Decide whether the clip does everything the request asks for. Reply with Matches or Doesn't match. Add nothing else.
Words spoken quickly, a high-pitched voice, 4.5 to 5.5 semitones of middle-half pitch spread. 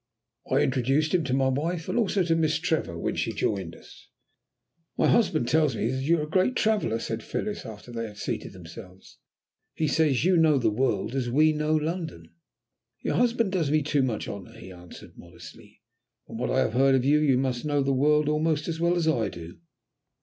Doesn't match